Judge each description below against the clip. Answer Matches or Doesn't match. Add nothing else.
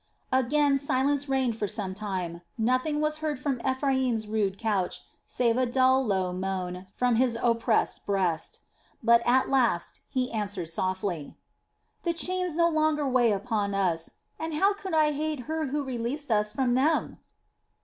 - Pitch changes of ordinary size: Doesn't match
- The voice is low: Doesn't match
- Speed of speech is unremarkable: Matches